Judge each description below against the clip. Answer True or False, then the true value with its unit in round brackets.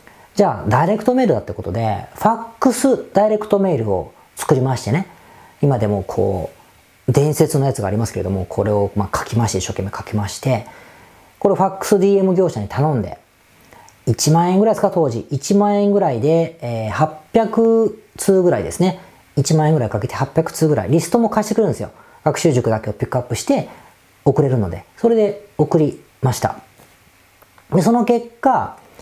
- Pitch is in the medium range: True (155 Hz)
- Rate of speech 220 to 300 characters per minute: False (350 characters per minute)